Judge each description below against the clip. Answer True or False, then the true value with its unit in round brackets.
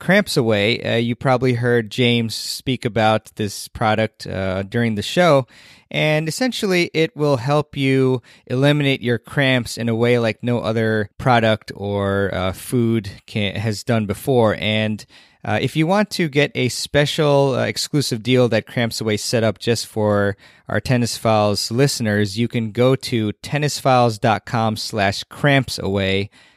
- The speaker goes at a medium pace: True (150 wpm)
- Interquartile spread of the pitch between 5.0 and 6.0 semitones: False (3.9 semitones)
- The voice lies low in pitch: True (120 Hz)